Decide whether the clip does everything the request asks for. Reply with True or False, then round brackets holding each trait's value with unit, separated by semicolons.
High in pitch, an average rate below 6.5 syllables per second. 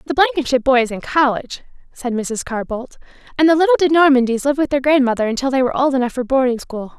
False (270 Hz; 6.7 syllables/s)